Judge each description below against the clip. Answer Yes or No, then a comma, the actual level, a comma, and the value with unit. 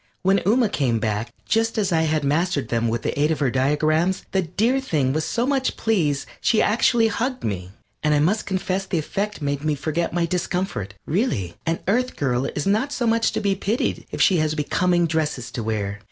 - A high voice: No, medium, 165 Hz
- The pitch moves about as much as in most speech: No, wide, 6.4 semitones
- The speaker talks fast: Yes, fast, 210 wpm